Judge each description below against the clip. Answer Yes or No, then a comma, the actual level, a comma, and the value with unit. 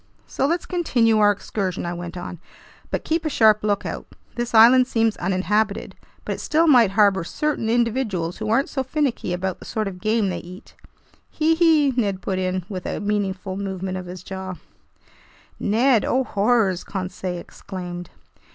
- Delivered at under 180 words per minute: Yes, average, 170 wpm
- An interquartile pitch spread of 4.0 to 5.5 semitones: Yes, average, 4.5 semitones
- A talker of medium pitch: No, high, 205 Hz